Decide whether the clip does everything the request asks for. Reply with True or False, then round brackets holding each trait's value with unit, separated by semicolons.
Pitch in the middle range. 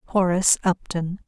True (180 Hz)